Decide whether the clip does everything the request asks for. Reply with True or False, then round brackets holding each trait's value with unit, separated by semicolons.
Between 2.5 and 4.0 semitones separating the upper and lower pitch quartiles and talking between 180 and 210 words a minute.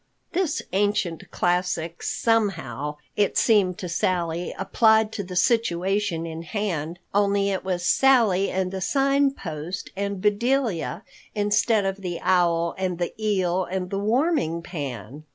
False (3.4 semitones; 135 wpm)